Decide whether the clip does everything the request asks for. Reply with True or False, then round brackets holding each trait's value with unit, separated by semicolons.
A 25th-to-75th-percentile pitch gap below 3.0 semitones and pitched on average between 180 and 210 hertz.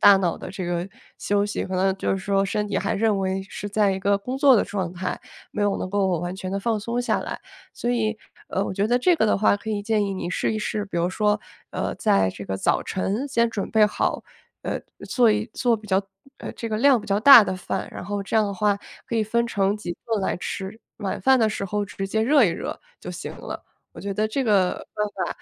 True (2.4 semitones; 205 Hz)